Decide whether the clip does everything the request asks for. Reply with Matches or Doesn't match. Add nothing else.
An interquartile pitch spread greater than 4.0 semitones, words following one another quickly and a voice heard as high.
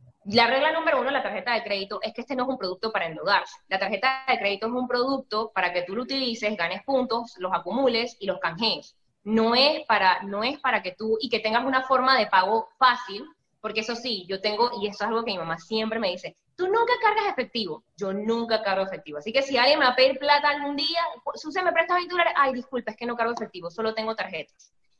Matches